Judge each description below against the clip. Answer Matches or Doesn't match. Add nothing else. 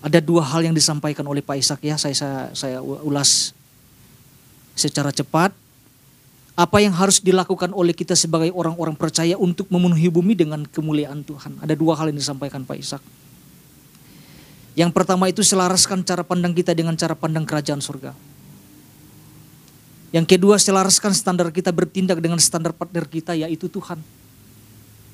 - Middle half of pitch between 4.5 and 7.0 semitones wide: Doesn't match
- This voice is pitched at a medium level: Matches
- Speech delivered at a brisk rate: Matches